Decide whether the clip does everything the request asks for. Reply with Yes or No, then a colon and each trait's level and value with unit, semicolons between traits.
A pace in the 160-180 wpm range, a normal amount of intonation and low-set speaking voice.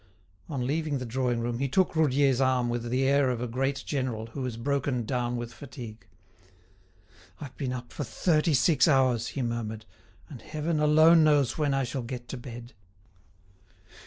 Yes: average, 175 wpm; average, 3.0 semitones; low, 130 Hz